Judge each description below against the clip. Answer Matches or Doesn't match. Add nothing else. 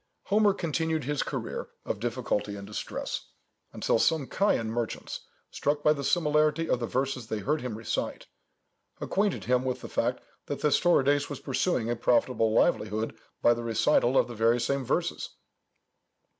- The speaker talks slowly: Doesn't match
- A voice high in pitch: Doesn't match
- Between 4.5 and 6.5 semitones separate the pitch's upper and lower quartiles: Matches